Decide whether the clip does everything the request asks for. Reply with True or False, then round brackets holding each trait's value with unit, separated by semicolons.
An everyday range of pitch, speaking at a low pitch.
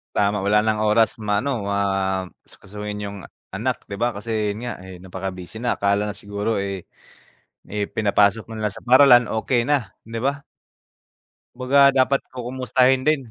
True (3.4 semitones; 105 Hz)